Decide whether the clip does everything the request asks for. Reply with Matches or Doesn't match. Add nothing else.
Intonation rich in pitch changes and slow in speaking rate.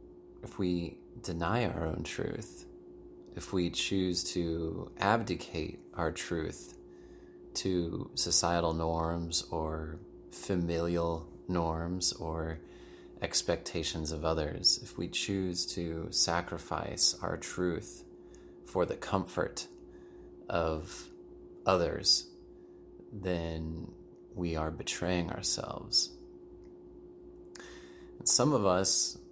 Doesn't match